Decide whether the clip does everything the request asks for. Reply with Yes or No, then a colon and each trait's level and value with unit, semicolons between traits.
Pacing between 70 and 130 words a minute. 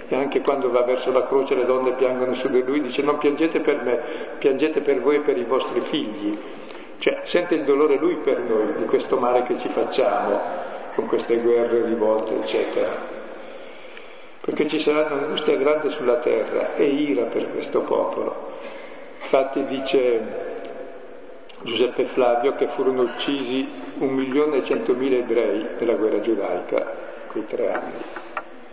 No: average, 160 wpm